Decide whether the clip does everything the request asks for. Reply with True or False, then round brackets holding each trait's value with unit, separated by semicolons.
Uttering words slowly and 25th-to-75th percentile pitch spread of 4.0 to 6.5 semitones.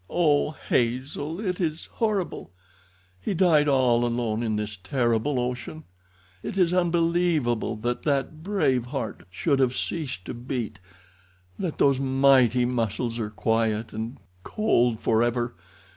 True (125 wpm; 5.3 semitones)